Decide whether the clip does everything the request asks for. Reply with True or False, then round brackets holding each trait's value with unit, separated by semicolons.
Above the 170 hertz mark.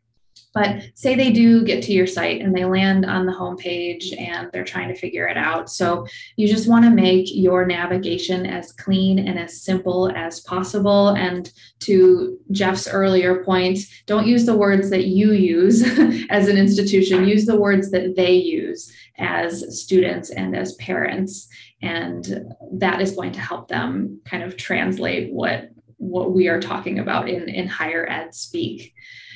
True (190 Hz)